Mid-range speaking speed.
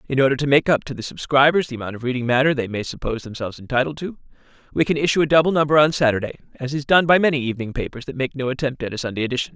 No: fast, 265 wpm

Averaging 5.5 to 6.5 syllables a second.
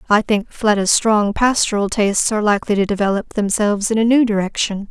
Yes: 6.3 syllables/s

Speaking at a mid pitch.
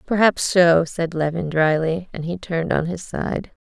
Yes: medium, 170 Hz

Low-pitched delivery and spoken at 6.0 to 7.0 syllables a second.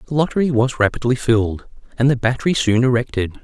Yes: low, 125 Hz; 6.6 syllables/s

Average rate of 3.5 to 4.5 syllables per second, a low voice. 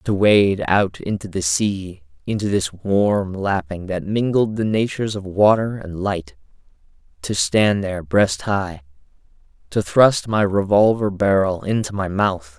Yes: 4.1 syllables/s; very low, 95 Hz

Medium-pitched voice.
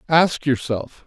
Yes: medium, 145 Hz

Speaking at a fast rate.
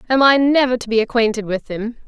Yes: fast, 230 wpm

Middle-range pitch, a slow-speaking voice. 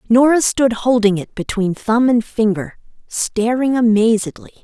No: high, 225 Hz; slow, 130 wpm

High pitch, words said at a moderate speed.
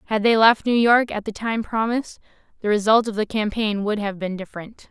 No: high, 215 Hz; fast, 220 wpm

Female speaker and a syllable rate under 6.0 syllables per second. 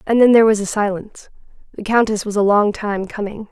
No: female; 6.1 syllables/s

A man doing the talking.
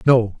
Yes: male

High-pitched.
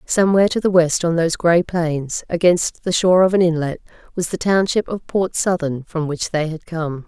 No: medium, 170 Hz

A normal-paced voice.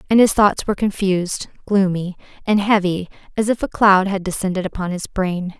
Yes: average, 180 wpm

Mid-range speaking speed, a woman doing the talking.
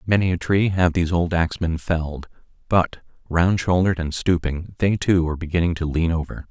No: average, 185 wpm; male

